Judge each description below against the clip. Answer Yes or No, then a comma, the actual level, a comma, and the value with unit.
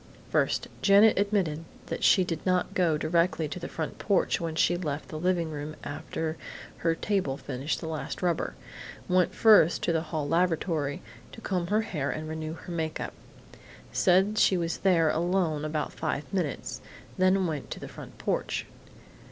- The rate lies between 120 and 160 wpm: No, average, 170 wpm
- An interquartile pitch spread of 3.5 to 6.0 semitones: No, average, 2.9 semitones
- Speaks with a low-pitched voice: No, medium, 165 Hz